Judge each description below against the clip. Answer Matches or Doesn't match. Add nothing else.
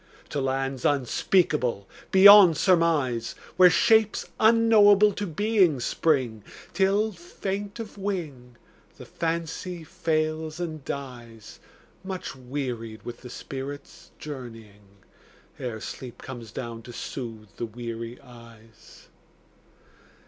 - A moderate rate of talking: Doesn't match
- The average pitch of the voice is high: Doesn't match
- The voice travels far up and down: Matches